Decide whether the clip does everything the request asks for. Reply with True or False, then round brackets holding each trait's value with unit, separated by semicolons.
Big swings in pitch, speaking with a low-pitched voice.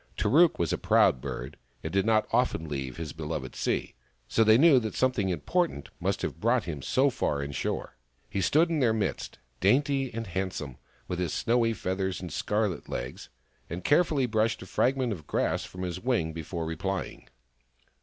True (7.0 semitones; 100 Hz)